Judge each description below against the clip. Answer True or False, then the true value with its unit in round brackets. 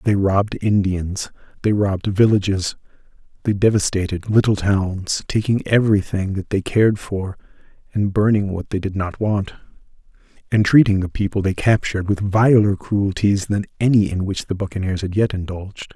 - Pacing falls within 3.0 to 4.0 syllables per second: False (5.1 syllables/s)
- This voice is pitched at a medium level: False (100 Hz)